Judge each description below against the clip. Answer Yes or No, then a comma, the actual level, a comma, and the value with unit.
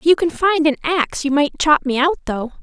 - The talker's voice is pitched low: No, very high, 300 Hz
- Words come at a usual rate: No, fast, 275 wpm